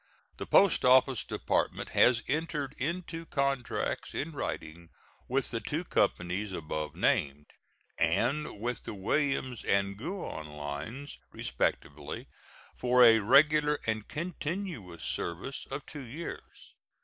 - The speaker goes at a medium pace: No, slow, 115 wpm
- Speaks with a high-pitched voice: No, low, 125 Hz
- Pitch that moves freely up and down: Yes, wide, 7.6 semitones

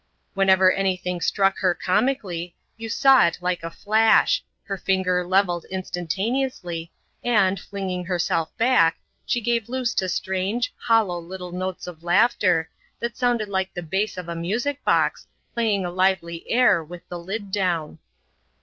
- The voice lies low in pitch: No, high, 190 Hz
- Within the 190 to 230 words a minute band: No, average, 155 wpm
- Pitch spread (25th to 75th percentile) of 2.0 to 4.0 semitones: Yes, average, 3.7 semitones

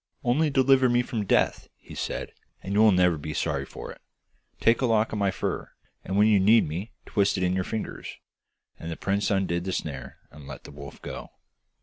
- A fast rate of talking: Yes, fast, 215 wpm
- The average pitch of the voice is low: Yes, low, 100 Hz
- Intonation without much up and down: No, average, 4.5 semitones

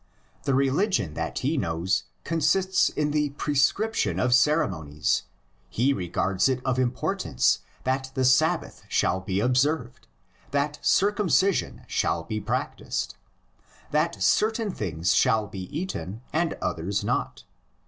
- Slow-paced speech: Yes, slow, 120 wpm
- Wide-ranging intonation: Yes, wide, 8.0 semitones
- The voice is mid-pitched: No, low, 130 Hz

